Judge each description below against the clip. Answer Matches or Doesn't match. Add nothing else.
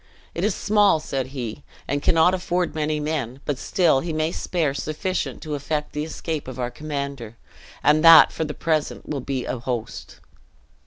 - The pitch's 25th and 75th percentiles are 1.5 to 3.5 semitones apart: Matches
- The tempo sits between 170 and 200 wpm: Matches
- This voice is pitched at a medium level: Matches